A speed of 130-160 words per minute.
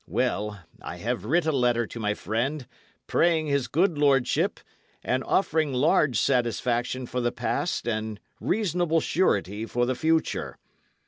Yes: average, 140 wpm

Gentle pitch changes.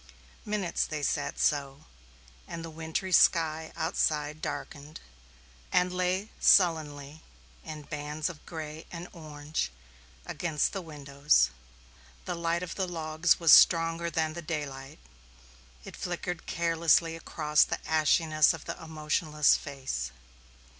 Yes: narrow, 2.1 semitones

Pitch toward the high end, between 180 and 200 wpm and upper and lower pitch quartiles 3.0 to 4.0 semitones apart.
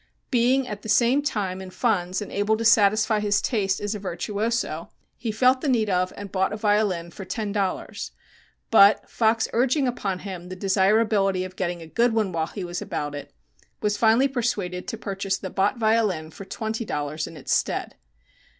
Yes: high, 205 Hz; average, 190 wpm; average, 3.4 semitones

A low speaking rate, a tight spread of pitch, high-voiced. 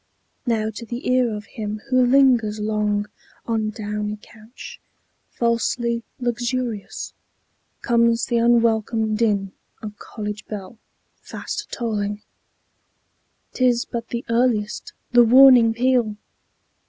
Yes: slow, 110 wpm; narrow, 2.2 semitones; high, 230 Hz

